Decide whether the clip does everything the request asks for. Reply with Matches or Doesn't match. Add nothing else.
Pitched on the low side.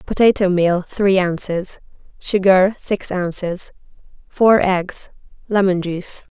Doesn't match